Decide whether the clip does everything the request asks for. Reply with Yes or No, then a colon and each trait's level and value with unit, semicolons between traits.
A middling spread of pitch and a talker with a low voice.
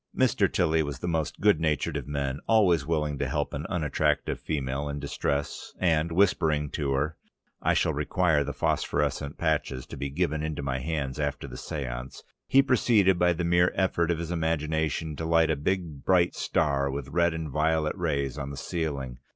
Yes: average, 3.1 semitones; very low, 75 Hz